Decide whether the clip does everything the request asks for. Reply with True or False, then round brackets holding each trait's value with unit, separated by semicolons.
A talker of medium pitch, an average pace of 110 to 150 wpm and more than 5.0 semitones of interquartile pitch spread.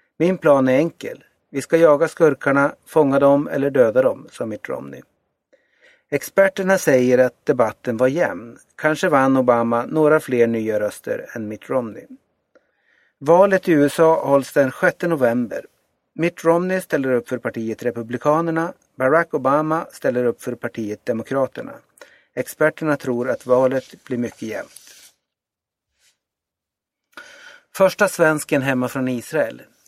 True (145 Hz; 130 wpm; 5.4 semitones)